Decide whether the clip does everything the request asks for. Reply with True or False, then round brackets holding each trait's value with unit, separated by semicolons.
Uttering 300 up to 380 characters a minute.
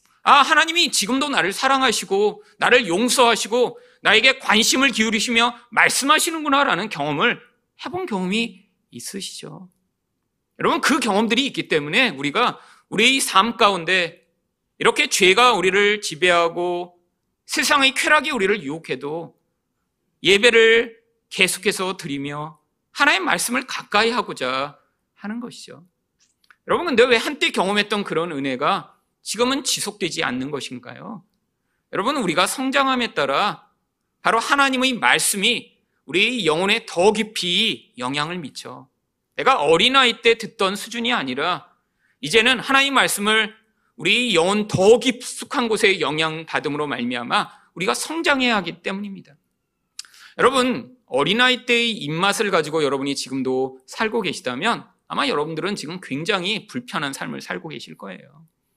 True (310 characters per minute)